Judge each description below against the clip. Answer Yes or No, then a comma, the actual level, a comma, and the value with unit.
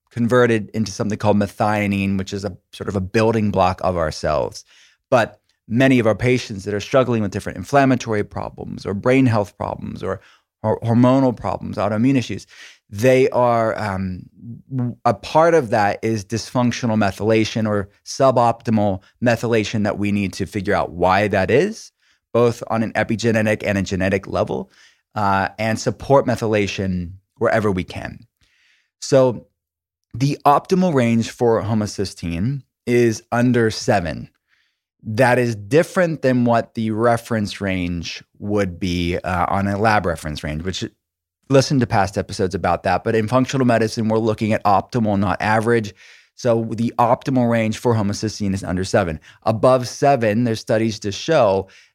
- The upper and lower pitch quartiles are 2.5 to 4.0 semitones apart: Yes, average, 3.2 semitones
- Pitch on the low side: Yes, low, 110 Hz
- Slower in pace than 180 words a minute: Yes, average, 150 wpm